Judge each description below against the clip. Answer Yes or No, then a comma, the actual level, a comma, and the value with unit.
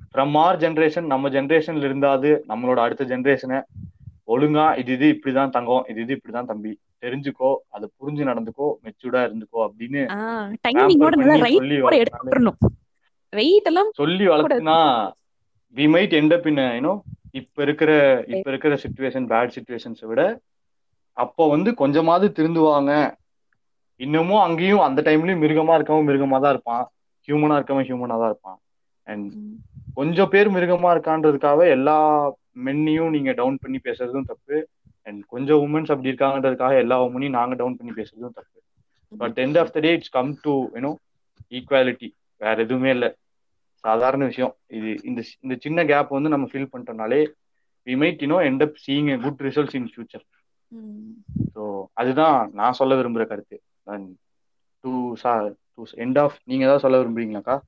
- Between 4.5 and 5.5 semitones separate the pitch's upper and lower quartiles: No, average, 3.8 semitones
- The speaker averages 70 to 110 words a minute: No, fast, 130 wpm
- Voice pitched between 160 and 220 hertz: No, low, 135 Hz